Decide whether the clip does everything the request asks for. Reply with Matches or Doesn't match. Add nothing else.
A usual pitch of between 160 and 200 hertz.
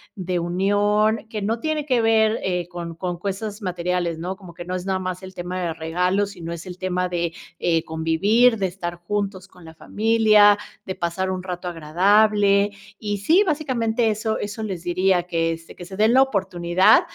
Matches